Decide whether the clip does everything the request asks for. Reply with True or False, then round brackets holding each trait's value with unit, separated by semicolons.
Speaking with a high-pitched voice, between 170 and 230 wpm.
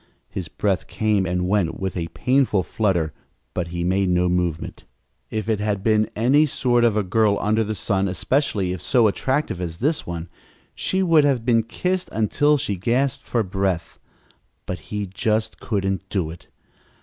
False (105 Hz; 175 wpm)